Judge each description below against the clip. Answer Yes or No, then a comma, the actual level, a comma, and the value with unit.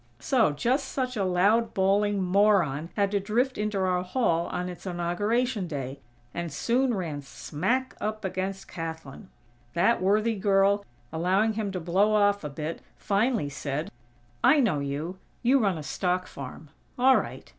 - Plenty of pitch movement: No, average, 4.2 semitones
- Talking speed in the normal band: Yes, average, 155 wpm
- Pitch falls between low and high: No, high, 195 Hz